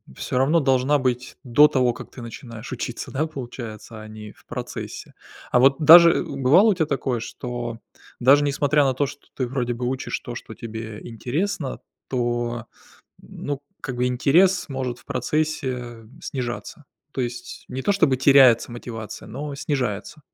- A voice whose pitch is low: Yes, low, 130 Hz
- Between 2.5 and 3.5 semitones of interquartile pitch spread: Yes, average, 3.1 semitones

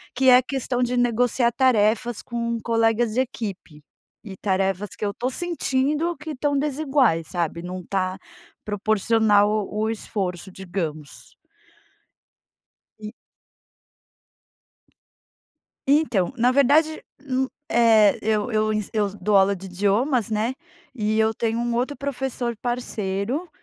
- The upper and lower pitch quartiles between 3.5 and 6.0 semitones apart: Yes, average, 4.1 semitones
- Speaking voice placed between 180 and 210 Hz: No, high, 225 Hz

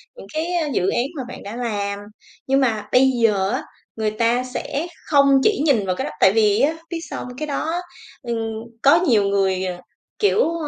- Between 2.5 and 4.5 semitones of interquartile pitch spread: No, wide, 5.6 semitones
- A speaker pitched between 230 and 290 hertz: Yes, high, 245 Hz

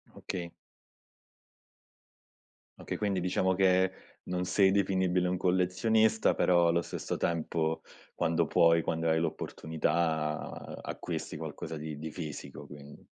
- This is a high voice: No, very low, 85 Hz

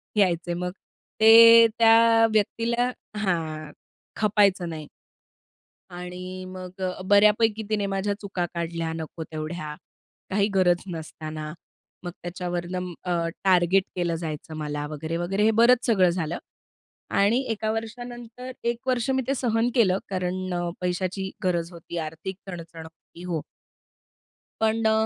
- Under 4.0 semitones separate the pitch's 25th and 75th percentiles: No, average, 4.4 semitones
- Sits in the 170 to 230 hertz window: Yes, medium, 185 Hz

